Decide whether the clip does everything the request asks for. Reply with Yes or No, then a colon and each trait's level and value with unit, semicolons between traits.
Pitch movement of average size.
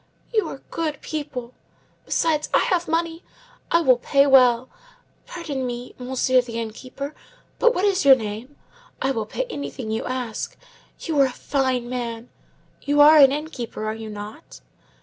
Yes: average, 4.2 semitones